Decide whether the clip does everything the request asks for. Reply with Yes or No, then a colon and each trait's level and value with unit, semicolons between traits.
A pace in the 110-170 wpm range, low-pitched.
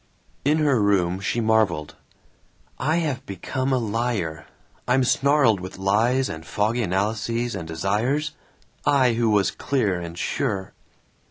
Yes: slow, 135 wpm; low, 110 Hz